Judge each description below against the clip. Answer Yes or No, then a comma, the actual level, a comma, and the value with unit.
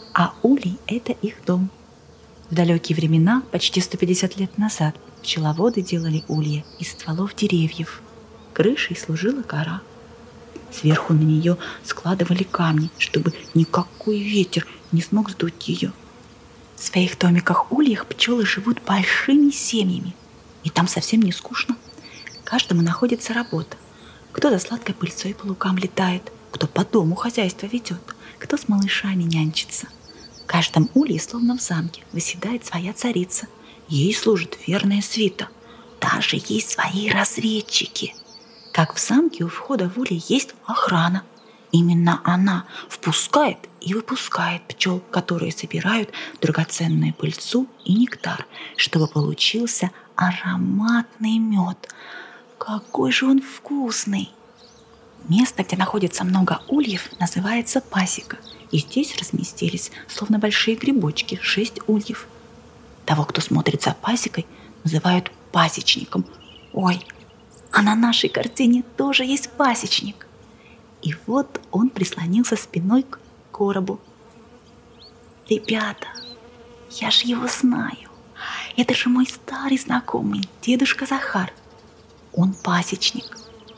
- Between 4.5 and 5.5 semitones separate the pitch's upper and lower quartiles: Yes, average, 4.9 semitones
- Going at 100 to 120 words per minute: Yes, average, 115 wpm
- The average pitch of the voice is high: Yes, high, 205 Hz